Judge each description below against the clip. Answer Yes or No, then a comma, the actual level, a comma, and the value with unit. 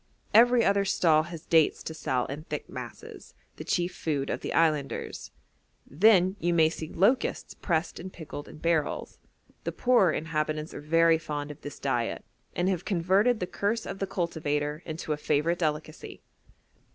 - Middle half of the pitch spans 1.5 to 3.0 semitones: No, average, 3.4 semitones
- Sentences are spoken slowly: No, average, 165 wpm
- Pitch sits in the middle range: Yes, medium, 165 Hz